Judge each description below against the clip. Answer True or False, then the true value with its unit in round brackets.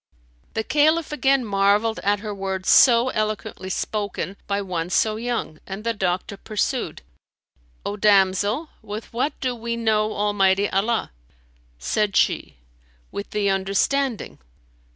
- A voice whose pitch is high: True (210 Hz)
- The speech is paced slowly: True (130 wpm)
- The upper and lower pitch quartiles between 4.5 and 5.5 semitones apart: False (2.9 semitones)